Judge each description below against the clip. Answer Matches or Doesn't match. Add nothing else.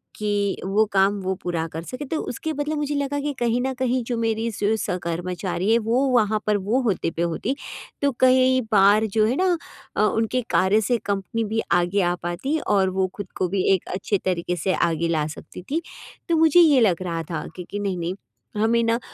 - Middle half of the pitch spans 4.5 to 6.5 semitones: Matches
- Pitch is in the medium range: Doesn't match